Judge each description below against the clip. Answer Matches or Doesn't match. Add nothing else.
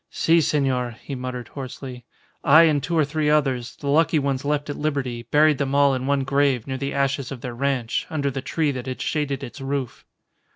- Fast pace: Matches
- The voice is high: Doesn't match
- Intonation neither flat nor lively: Doesn't match